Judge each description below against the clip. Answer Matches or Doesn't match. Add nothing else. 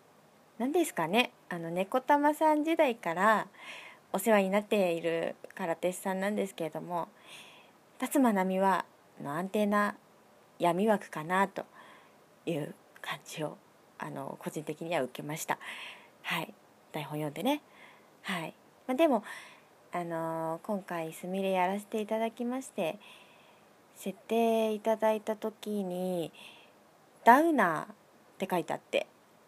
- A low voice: Doesn't match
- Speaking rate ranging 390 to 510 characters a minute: Doesn't match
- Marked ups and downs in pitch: Doesn't match